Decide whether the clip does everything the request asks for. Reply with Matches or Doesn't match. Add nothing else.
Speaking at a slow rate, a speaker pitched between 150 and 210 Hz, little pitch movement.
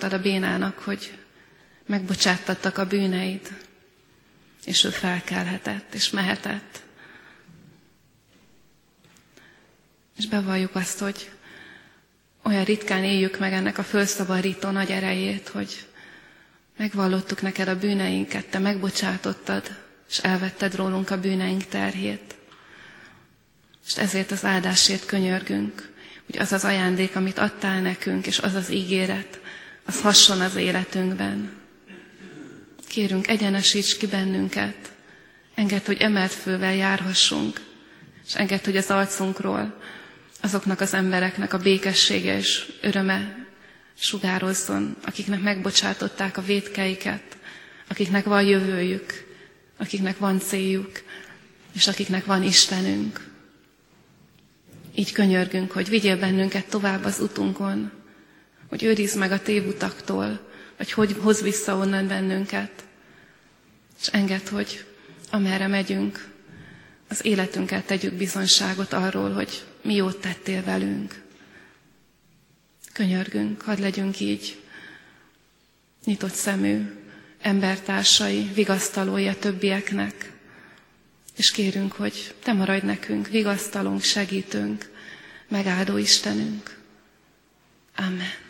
Matches